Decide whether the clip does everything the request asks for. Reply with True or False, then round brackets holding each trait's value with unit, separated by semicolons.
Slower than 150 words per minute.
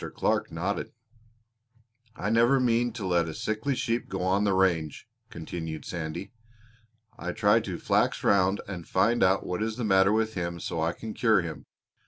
False (175 wpm)